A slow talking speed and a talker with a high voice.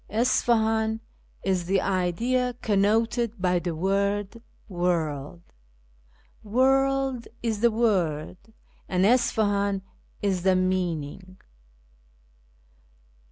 Yes: slow, 95 wpm; high, 200 Hz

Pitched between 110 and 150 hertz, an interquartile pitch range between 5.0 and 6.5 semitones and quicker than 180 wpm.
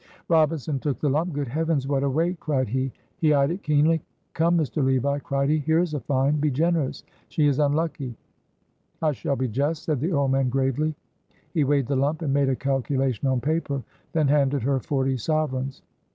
No: medium, 140 Hz; narrow, 2.6 semitones; average, 195 wpm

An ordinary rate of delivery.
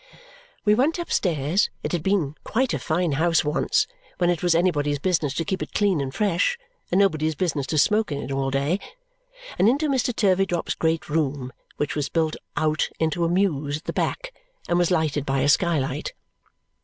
Yes: average, 190 wpm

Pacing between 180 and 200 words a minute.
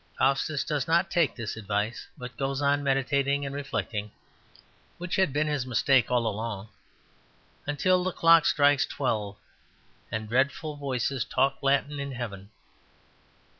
No: slow, 135 wpm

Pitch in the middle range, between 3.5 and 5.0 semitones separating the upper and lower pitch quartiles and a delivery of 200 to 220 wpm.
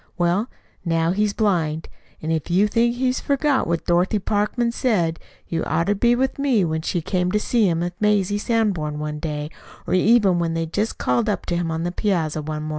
Yes: medium, 180 Hz; average, 4.6 semitones; fast, 205 wpm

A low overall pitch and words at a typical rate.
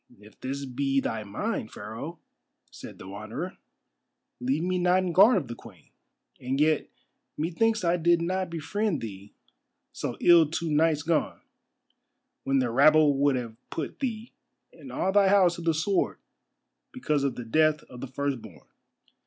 No: medium, 155 Hz; average, 160 wpm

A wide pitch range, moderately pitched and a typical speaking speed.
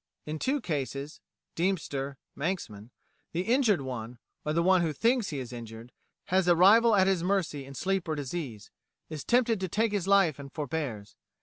Yes: wide, 6.0 semitones; medium, 165 Hz; average, 180 wpm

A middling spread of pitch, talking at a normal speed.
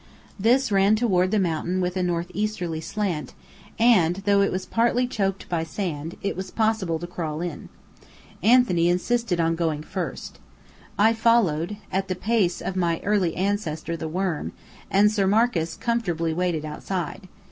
Yes: average, 4.0 semitones; average, 155 wpm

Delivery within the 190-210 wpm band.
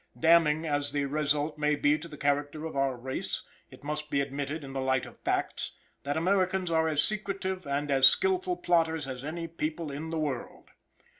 Yes: average, 195 wpm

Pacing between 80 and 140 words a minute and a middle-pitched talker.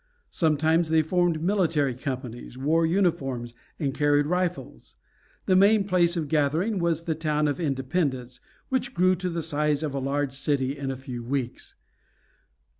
No: average, 155 wpm; medium, 150 Hz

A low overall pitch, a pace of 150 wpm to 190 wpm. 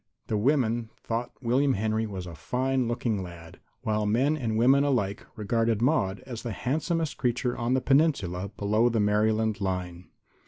Yes: low, 115 Hz; average, 155 wpm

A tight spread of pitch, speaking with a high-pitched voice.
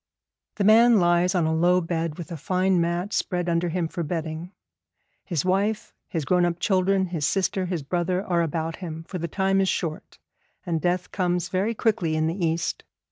No: narrow, 2.2 semitones; medium, 175 Hz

